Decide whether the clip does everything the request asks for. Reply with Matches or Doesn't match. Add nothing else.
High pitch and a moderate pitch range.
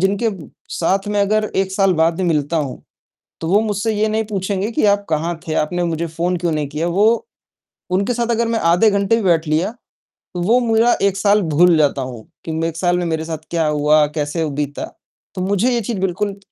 Doesn't match